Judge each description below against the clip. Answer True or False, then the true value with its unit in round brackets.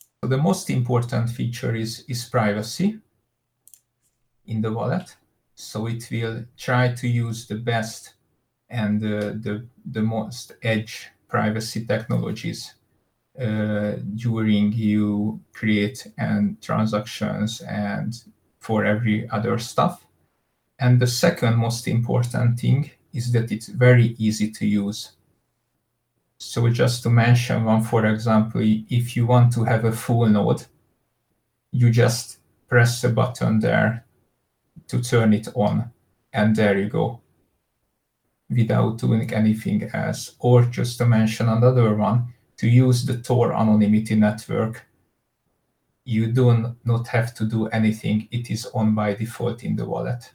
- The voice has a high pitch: False (115 Hz)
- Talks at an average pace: False (130 wpm)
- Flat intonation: True (2.1 semitones)